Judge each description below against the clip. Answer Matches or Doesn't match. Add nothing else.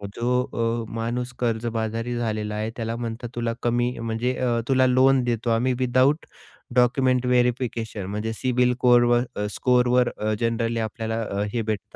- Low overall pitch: Matches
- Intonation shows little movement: Matches